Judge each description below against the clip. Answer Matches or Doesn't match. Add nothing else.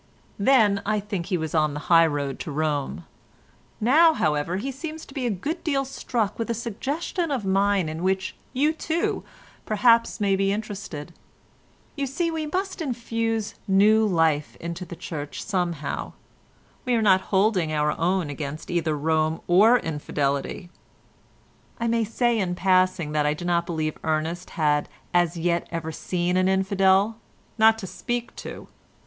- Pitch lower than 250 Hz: Matches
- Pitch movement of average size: Doesn't match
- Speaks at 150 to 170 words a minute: Matches